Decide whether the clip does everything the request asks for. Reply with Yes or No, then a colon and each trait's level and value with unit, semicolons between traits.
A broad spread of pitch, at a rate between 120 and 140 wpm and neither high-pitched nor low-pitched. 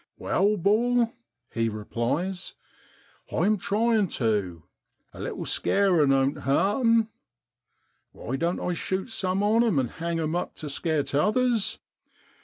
Yes: wide, 7.4 semitones; slow, 135 wpm; medium, 180 Hz